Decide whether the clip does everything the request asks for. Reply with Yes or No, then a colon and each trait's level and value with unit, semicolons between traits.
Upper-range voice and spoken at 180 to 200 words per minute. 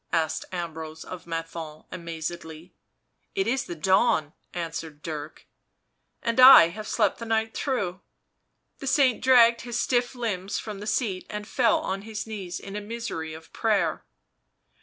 No: high, 195 Hz; average, 155 wpm